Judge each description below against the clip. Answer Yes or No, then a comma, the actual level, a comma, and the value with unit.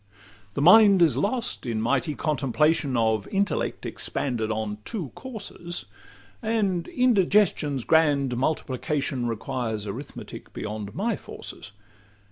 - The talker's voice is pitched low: No, medium, 145 Hz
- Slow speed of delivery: Yes, slow, 105 wpm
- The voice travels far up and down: Yes, wide, 8.2 semitones